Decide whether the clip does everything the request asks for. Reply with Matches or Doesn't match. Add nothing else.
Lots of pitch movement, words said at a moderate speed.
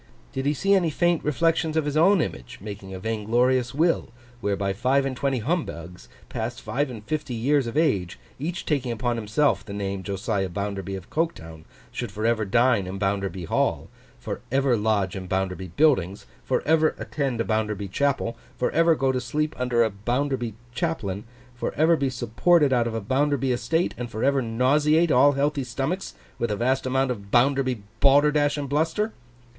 Matches